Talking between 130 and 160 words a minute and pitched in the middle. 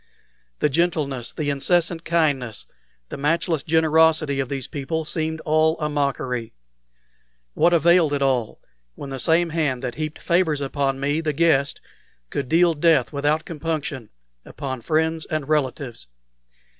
Yes: average, 140 wpm; medium, 150 Hz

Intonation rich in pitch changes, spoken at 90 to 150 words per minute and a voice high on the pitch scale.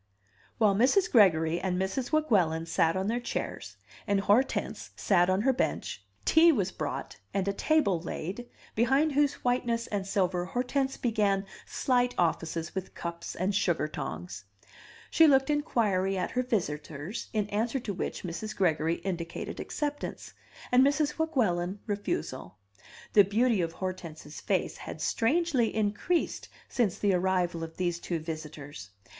Yes: wide, 6.2 semitones; average, 145 wpm; high, 200 Hz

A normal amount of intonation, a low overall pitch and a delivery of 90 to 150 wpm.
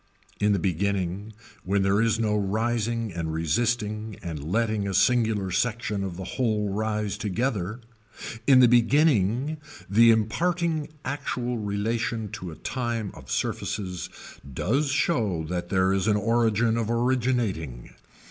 Yes: average, 3.4 semitones; low, 110 Hz; slow, 135 wpm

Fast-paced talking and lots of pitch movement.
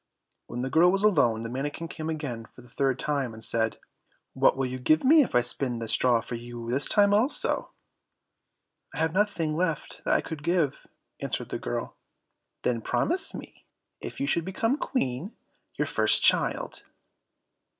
No: average, 175 wpm; wide, 6.8 semitones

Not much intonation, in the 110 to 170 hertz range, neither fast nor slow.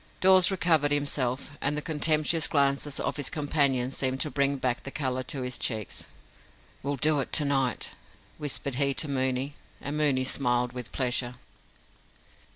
Yes: narrow, 2.3 semitones; medium, 140 Hz; average, 160 wpm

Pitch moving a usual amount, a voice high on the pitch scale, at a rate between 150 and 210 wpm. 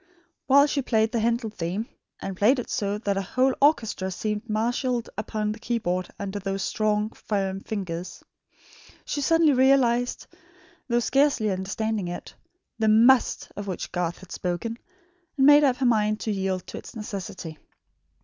Yes: average, 3.9 semitones; high, 215 Hz; average, 160 wpm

